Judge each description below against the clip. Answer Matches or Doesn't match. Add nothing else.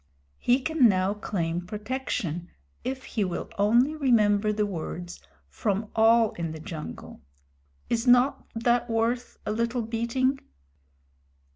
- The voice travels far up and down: Doesn't match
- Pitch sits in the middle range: Doesn't match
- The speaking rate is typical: Doesn't match